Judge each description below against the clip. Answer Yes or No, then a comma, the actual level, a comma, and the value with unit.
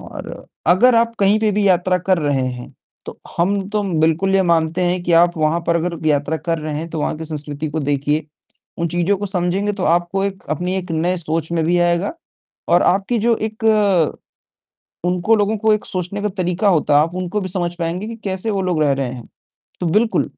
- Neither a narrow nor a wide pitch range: Yes, average, 3.7 semitones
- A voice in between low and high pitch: Yes, medium, 175 Hz